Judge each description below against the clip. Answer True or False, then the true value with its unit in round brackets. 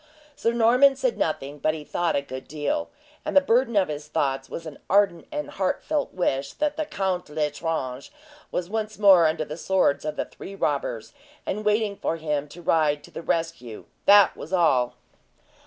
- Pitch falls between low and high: True (165 Hz)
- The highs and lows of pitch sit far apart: True (6.1 semitones)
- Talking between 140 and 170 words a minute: False (185 wpm)